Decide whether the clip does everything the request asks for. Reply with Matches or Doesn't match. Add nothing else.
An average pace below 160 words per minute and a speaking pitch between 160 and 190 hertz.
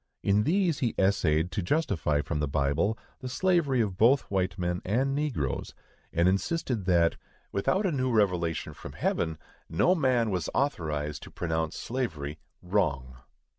Doesn't match